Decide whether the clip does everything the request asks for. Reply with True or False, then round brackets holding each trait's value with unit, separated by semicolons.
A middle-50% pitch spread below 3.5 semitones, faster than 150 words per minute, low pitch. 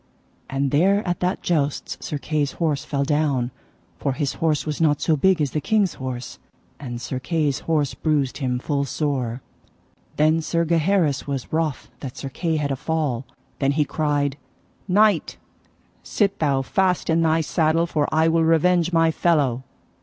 False (3.0 semitones; 170 wpm; 150 Hz)